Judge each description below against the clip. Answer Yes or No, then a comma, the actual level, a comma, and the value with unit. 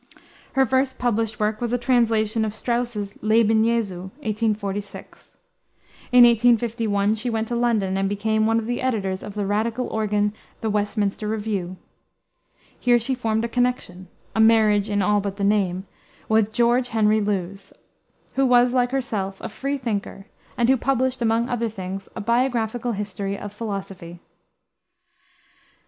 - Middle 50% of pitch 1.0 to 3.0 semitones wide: Yes, average, 2.7 semitones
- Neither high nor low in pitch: No, high, 220 Hz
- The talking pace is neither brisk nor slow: Yes, average, 150 wpm